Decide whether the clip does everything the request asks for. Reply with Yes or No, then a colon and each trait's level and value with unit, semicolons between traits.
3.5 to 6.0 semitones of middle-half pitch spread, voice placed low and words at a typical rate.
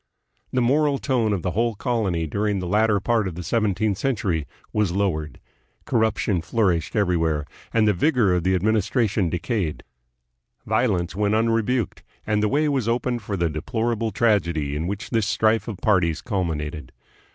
Yes: average, 4.4 semitones; low, 105 Hz; average, 165 wpm